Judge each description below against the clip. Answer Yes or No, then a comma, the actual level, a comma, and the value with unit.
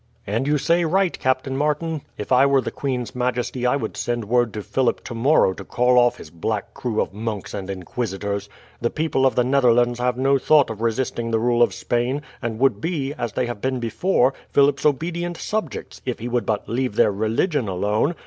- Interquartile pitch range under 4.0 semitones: Yes, average, 3.6 semitones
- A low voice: Yes, low, 125 Hz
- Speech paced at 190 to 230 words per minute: Yes, fast, 205 wpm